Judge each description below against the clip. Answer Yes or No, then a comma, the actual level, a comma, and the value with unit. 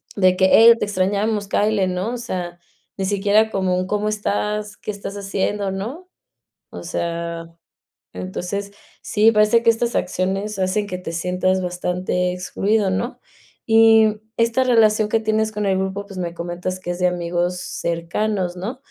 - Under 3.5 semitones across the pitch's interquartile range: Yes, average, 2.9 semitones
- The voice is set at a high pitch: Yes, high, 195 Hz